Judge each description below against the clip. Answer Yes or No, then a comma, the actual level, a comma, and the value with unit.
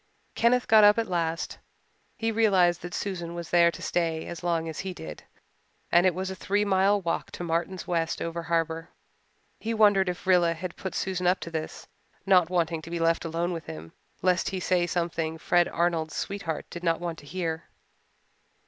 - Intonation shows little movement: Yes, narrow, 2.2 semitones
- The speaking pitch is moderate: Yes, medium, 175 Hz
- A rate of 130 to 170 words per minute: No, average, 195 wpm